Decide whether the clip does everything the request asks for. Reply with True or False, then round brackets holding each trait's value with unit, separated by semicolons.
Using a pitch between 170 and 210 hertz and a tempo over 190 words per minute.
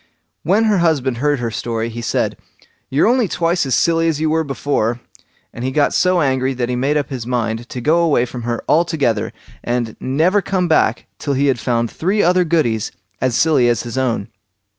False (135 Hz; 205 wpm)